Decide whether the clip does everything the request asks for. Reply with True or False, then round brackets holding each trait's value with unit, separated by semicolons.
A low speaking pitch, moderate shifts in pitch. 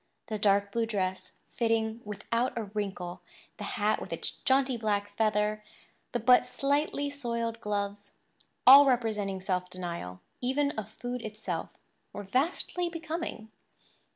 False (220 Hz; 3.6 semitones)